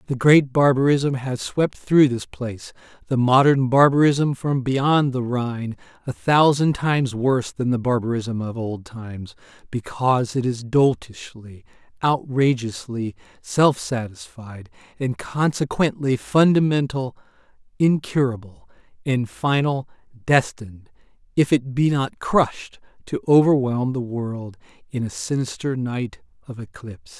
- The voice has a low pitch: Yes, low, 130 Hz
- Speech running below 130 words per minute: Yes, slow, 115 wpm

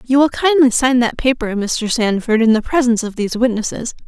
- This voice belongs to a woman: Yes, female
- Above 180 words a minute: Yes, fast, 205 wpm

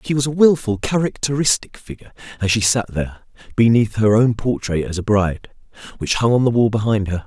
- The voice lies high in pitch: No, low, 115 Hz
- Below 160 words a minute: No, average, 200 wpm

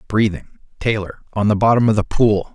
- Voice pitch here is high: No, low, 105 Hz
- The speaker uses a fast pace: No, average, 190 wpm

